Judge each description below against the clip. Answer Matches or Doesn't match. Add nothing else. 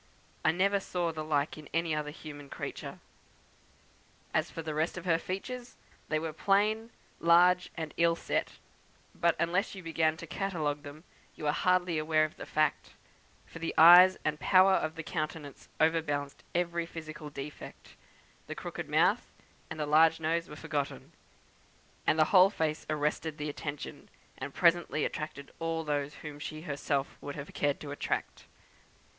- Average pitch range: Doesn't match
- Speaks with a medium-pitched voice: Matches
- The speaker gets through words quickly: Doesn't match